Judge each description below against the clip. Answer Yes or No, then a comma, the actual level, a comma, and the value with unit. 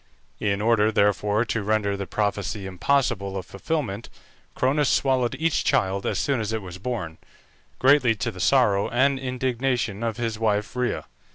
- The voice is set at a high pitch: No, low, 110 Hz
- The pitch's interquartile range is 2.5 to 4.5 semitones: Yes, average, 4.1 semitones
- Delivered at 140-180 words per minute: Yes, average, 160 wpm